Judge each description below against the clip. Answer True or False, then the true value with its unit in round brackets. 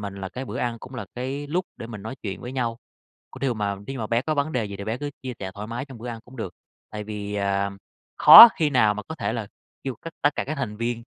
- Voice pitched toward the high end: False (115 Hz)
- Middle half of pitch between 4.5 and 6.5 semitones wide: False (4.1 semitones)